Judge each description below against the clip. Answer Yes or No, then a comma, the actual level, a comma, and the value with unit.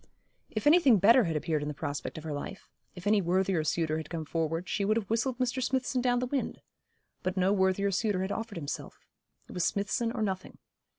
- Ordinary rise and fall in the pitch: No, wide, 5.7 semitones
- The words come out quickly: Yes, fast, 215 wpm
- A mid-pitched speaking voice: No, high, 195 Hz